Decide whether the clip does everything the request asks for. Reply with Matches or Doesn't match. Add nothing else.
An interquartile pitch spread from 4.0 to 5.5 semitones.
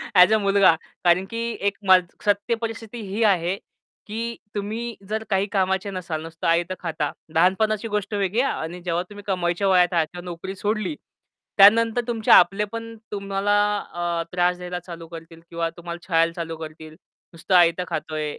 Doesn't match